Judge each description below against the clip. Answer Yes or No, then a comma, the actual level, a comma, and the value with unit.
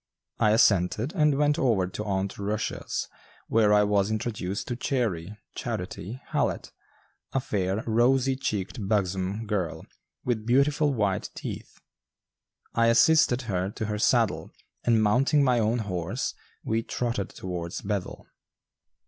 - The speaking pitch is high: No, low, 110 Hz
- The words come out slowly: Yes, slow, 130 wpm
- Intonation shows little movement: No, average, 3.8 semitones